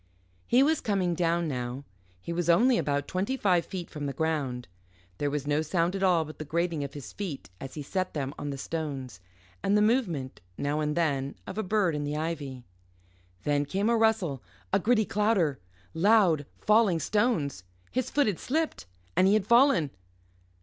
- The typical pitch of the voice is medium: Yes, medium, 170 Hz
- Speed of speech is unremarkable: Yes, average, 185 wpm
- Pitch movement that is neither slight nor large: No, wide, 6.3 semitones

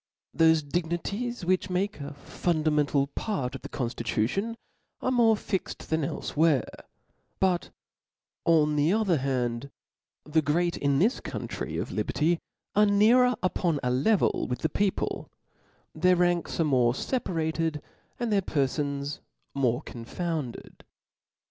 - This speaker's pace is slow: Yes, slow, 125 wpm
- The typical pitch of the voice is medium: Yes, medium, 160 Hz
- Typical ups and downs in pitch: Yes, average, 4.9 semitones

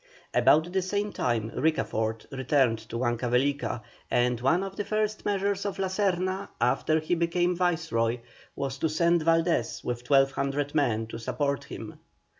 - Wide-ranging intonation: Yes, wide, 6.6 semitones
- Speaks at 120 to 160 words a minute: Yes, average, 150 wpm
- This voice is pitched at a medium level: Yes, medium, 150 Hz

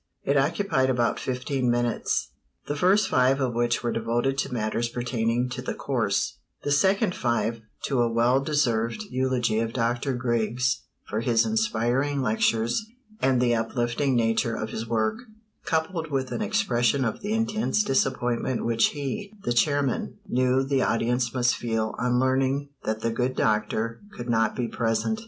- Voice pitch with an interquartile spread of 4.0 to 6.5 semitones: No, average, 2.8 semitones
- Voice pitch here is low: Yes, low, 125 Hz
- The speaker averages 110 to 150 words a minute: No, average, 160 wpm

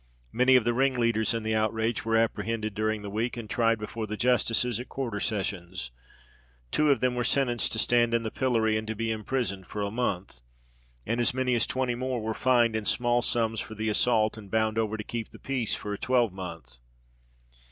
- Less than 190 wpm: No, fast, 205 wpm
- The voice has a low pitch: Yes, low, 115 Hz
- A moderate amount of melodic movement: No, narrow, 2.1 semitones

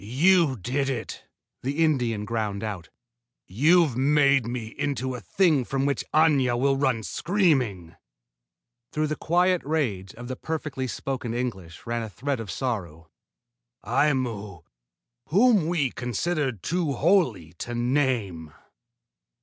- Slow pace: Yes, slow, 125 wpm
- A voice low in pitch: Yes, low, 130 Hz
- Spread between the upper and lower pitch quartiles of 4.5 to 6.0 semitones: Yes, average, 5.2 semitones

